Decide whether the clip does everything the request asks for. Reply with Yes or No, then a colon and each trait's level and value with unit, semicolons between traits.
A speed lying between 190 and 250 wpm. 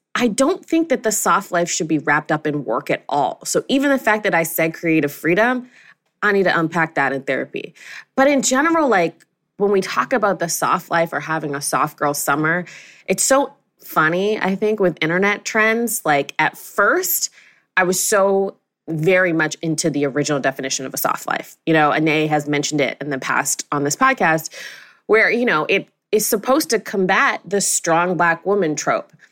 Yes: average, 200 wpm